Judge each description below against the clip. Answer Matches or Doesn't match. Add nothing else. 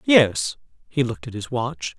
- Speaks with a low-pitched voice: Matches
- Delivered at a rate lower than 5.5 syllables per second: Matches